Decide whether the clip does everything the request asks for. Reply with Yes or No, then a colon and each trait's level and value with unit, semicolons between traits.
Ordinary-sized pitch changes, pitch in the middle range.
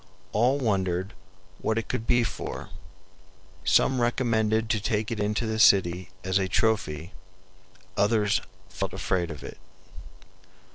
No: average, 3.3 semitones; low, 105 Hz